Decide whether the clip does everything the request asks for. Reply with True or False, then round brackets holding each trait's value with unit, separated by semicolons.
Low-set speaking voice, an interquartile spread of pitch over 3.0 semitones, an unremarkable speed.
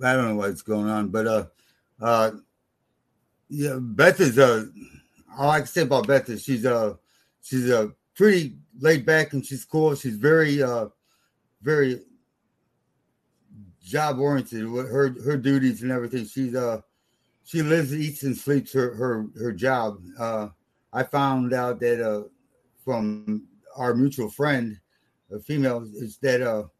True (125 Hz; 4.2 semitones; 150 wpm)